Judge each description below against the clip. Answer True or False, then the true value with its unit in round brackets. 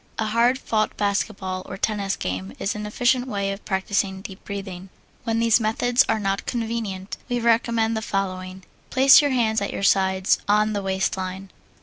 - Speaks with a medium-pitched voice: False (205 Hz)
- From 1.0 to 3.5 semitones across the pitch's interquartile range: True (3.0 semitones)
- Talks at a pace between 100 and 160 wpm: False (180 wpm)